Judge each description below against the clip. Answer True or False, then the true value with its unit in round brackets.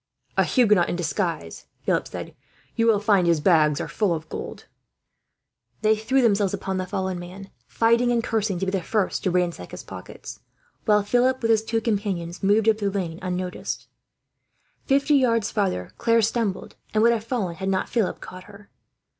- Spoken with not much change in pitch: False (3.8 semitones)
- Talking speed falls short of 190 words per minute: True (180 wpm)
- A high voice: True (200 Hz)